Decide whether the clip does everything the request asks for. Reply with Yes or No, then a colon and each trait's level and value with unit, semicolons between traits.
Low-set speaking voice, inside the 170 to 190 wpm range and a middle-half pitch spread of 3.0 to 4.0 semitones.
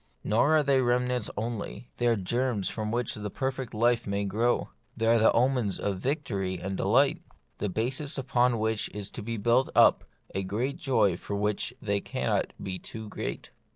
Yes: low, 115 Hz; average, 180 wpm; average, 3.6 semitones